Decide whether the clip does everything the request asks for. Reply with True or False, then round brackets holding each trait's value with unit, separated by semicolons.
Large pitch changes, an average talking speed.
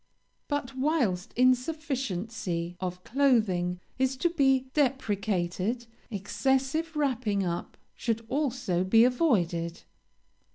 False (6.4 semitones; 90 wpm)